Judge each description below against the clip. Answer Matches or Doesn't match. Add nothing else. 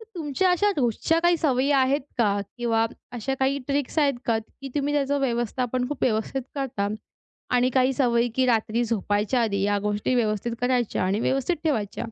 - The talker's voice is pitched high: Matches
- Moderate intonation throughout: Matches